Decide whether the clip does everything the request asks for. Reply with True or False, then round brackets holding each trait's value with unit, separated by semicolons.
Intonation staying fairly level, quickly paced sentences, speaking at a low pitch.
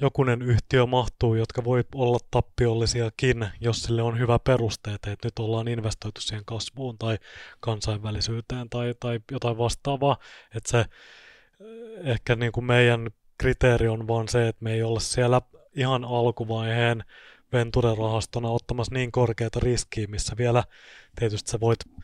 False (1.5 semitones; 140 wpm; 115 Hz)